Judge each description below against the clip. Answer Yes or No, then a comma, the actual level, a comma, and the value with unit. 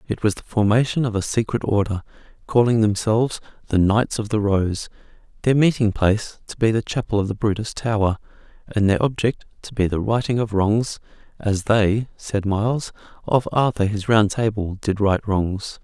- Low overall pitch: Yes, low, 105 Hz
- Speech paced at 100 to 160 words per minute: No, average, 180 wpm